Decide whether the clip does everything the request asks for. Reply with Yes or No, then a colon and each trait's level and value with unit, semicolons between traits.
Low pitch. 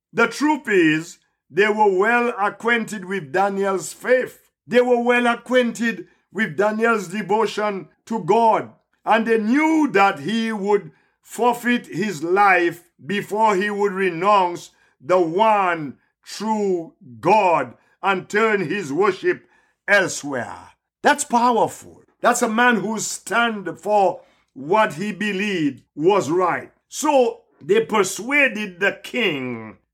No: high, 215 Hz